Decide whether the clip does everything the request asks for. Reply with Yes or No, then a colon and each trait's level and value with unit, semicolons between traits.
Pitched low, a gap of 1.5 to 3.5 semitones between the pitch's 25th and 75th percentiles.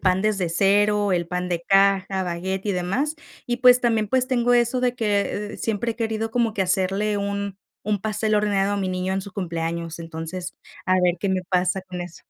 No: high, 195 Hz; average, 2.8 semitones